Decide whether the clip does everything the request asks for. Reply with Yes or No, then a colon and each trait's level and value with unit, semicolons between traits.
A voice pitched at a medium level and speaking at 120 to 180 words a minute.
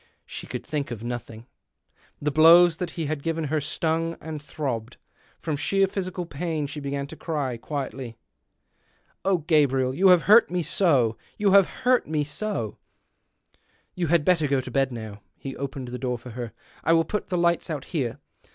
No: medium, 150 Hz; average, 195 wpm